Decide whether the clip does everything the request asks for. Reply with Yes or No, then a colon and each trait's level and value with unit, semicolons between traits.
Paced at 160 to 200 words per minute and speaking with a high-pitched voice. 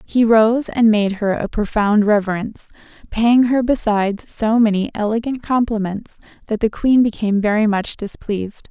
No: average, 150 wpm; high, 220 Hz